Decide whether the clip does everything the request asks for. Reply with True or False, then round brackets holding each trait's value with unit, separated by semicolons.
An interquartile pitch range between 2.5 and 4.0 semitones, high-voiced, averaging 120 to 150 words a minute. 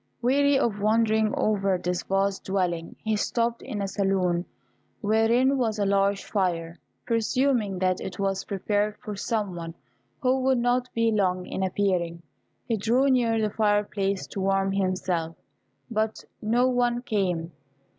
True (3.3 semitones; 205 Hz; 145 wpm)